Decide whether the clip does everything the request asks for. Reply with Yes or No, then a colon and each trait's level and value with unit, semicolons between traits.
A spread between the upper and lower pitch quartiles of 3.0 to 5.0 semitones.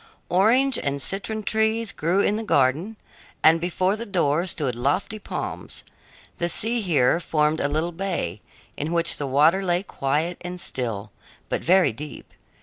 No: wide, 5.4 semitones